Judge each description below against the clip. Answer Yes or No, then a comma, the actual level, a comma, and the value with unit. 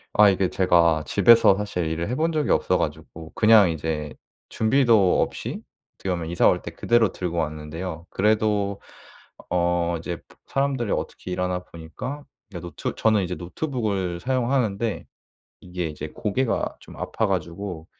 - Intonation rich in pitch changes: No, average, 4.5 semitones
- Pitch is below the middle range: Yes, very low, 90 Hz